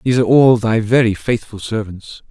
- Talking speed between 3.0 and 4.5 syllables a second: No, 5.6 syllables/s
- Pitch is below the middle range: Yes, low, 115 Hz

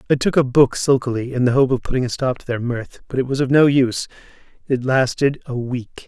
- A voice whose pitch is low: Yes, low, 130 Hz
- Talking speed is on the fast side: Yes, fast, 245 wpm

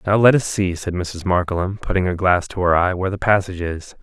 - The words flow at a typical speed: No, fast, 255 wpm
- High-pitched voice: No, very low, 90 Hz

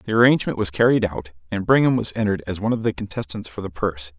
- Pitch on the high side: No, low, 100 Hz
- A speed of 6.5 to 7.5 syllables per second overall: Yes, 7.2 syllables/s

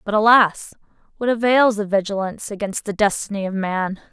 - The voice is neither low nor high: No, high, 205 Hz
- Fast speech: No, average, 160 wpm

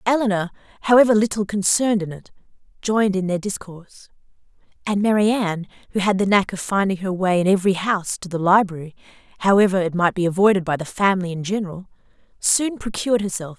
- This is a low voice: No, high, 195 Hz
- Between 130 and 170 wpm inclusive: No, average, 180 wpm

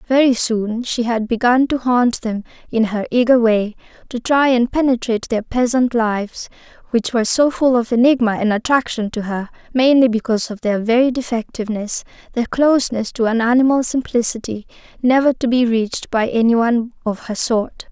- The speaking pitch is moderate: No, high, 235 Hz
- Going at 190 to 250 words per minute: No, average, 170 wpm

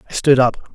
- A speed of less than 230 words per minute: No, fast, 240 wpm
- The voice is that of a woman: No, male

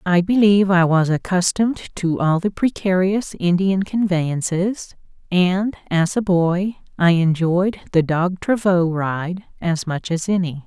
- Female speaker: Yes, female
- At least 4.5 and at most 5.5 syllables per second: No, 4.0 syllables/s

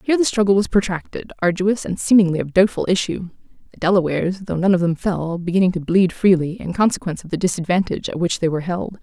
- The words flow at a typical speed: No, fast, 215 wpm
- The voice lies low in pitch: No, medium, 185 Hz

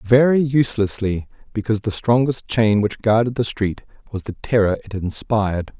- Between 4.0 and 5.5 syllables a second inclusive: Yes, 5.1 syllables/s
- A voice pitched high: No, low, 110 Hz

